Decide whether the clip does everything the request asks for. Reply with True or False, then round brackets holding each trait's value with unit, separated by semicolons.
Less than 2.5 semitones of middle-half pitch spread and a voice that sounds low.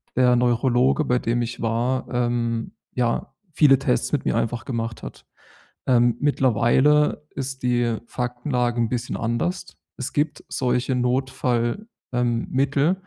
True (2.0 semitones; 125 Hz)